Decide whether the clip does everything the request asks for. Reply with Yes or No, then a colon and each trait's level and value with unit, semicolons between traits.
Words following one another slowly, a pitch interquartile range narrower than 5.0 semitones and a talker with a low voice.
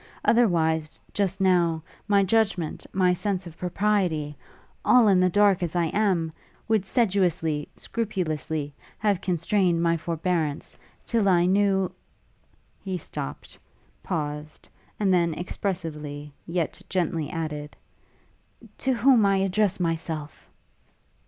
No: slow, 115 wpm; average, 3.7 semitones; medium, 180 Hz